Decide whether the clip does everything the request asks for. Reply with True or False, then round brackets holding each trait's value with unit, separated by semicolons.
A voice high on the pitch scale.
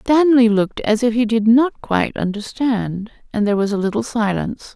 True (225 Hz)